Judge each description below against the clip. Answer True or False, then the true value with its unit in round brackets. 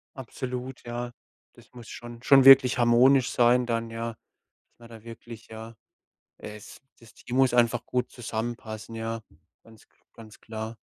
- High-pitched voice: False (120 Hz)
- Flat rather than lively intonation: True (1.6 semitones)